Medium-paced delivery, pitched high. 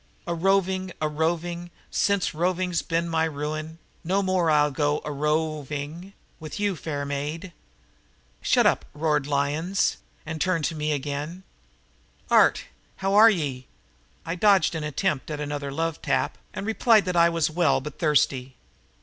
No: average, 165 wpm; medium, 160 Hz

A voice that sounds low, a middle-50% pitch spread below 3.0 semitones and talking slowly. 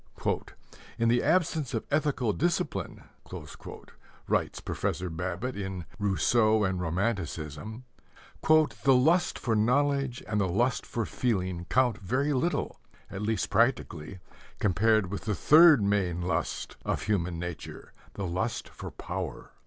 No: low, 110 Hz; wide, 5.6 semitones; slow, 125 wpm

